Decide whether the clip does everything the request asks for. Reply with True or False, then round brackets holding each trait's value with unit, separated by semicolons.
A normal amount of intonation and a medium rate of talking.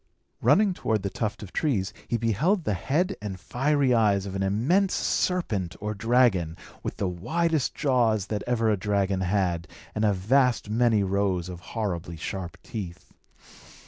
True (4.8 semitones; 160 wpm)